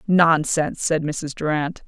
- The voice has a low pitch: No, medium, 155 Hz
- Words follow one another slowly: Yes, slow, 130 wpm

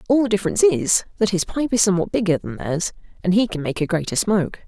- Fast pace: Yes, fast, 245 wpm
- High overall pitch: Yes, high, 195 Hz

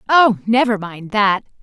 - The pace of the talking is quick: No, average, 150 wpm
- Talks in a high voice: Yes, high, 215 Hz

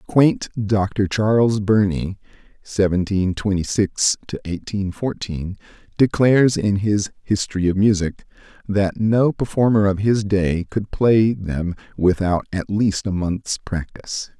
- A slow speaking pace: Yes, slow, 130 wpm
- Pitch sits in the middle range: No, low, 100 Hz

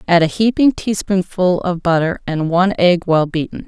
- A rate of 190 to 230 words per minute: No, average, 180 wpm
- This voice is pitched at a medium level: Yes, medium, 180 Hz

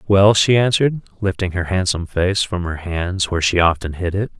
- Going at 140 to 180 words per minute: No, fast, 205 wpm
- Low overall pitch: Yes, very low, 95 Hz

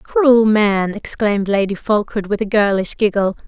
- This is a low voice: No, high, 205 Hz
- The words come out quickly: No, average, 155 wpm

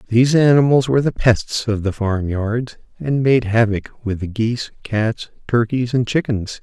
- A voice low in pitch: Yes, low, 115 Hz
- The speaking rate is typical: Yes, average, 170 wpm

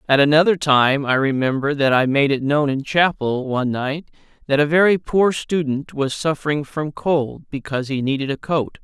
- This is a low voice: No, medium, 145 Hz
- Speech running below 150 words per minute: No, average, 190 wpm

